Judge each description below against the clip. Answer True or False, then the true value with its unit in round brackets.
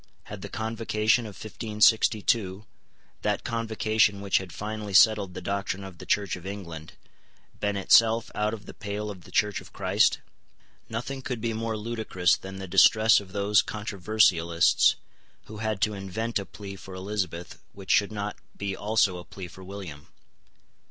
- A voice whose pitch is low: True (105 Hz)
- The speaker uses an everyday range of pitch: False (2.3 semitones)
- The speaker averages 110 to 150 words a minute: False (165 wpm)